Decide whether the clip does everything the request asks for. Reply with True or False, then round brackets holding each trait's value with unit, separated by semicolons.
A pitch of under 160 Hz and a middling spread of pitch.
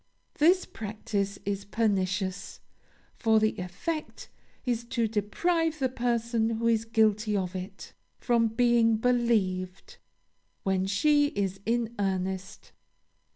False (220 Hz; 3.4 semitones)